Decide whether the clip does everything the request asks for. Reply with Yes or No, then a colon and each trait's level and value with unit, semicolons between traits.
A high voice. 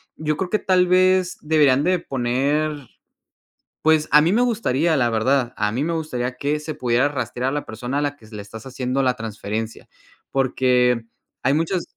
No: medium, 140 Hz